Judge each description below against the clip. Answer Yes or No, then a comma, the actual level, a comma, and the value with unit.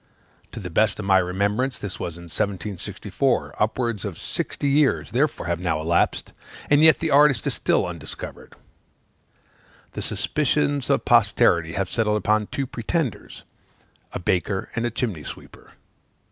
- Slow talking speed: No, average, 145 wpm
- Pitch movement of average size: No, wide, 6.3 semitones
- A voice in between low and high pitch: No, low, 105 Hz